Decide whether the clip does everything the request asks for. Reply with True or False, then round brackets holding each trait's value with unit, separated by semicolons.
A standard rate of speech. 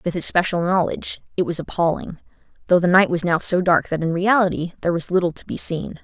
False (220 wpm)